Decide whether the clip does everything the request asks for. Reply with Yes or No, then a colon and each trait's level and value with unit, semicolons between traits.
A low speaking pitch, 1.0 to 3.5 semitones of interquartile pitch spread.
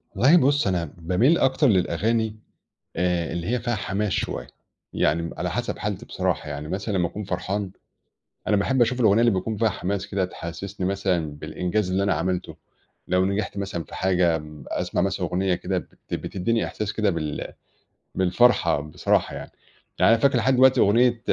No: very low, 95 Hz; average, 4.1 semitones